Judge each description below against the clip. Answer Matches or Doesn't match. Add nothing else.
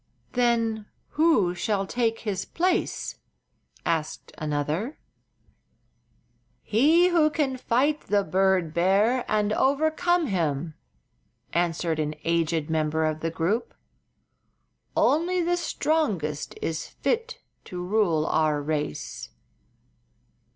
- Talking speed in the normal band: Doesn't match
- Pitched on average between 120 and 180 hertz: Doesn't match